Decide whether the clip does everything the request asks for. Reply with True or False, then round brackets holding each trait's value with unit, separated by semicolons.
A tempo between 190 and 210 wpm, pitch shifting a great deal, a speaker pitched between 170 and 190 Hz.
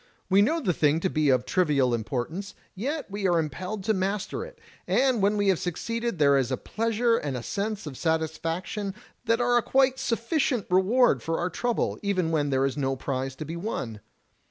True (200 wpm; 7.4 semitones; 185 Hz)